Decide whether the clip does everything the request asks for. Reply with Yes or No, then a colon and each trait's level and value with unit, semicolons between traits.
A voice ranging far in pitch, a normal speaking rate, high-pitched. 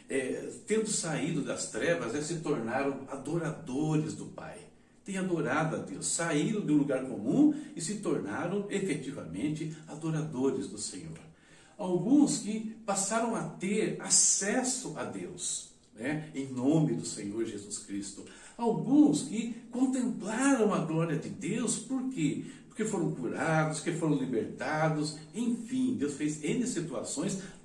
No: wide, 6.7 semitones; average, 130 wpm; medium, 170 Hz